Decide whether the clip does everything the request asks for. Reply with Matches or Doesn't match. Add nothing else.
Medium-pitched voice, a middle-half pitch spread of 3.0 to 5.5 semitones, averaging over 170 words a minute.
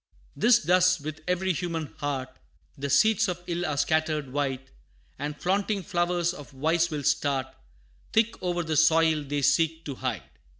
Doesn't match